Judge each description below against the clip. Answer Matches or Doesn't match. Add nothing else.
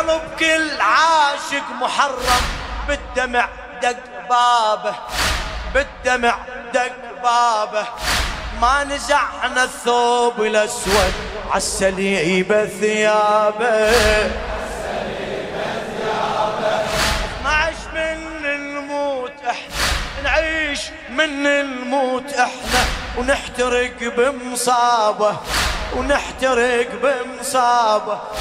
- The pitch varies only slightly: Doesn't match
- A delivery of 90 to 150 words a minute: Doesn't match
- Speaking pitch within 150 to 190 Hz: Doesn't match